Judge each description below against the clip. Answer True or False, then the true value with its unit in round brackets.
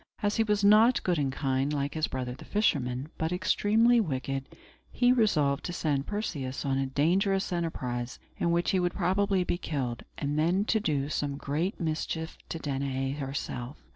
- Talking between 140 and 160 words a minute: False (175 wpm)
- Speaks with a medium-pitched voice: True (155 Hz)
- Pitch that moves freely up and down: True (5.9 semitones)